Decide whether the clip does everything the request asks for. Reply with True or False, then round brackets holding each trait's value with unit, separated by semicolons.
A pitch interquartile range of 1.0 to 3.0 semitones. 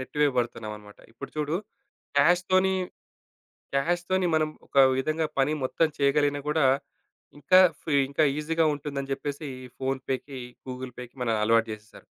False (3.4 semitones)